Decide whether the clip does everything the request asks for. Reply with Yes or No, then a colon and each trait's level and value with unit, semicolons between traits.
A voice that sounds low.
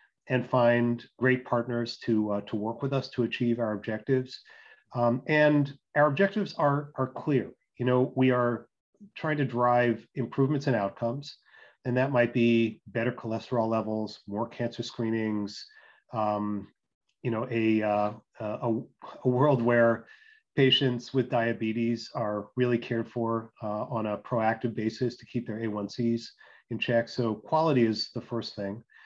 Yes: low, 120 Hz